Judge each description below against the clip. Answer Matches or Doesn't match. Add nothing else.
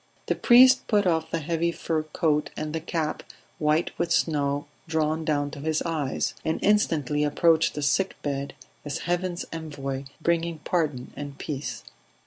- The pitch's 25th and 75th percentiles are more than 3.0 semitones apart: Doesn't match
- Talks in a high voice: Doesn't match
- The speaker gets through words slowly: Doesn't match